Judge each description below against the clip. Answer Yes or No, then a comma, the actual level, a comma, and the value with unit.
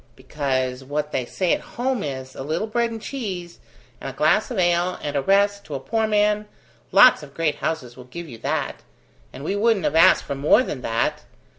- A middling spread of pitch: No, wide, 7.2 semitones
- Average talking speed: No, fast, 210 wpm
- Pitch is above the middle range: No, medium, 165 Hz